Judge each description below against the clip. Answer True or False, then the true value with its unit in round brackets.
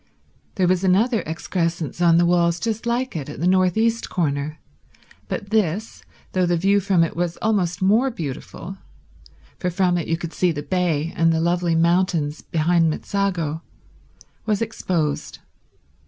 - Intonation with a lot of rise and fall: False (2.9 semitones)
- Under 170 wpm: True (155 wpm)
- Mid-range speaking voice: True (175 Hz)